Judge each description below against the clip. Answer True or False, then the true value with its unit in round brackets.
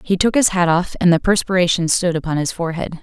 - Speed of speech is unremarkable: False (240 wpm)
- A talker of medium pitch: True (175 Hz)